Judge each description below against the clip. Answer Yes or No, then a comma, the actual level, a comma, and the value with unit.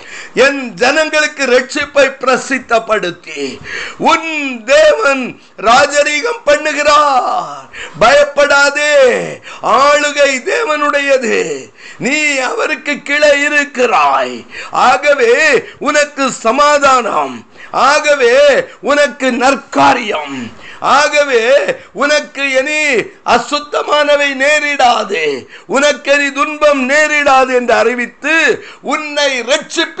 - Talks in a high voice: Yes, very high, 290 Hz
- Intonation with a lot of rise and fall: No, narrow, 2.4 semitones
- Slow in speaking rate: Yes, slow, 70 wpm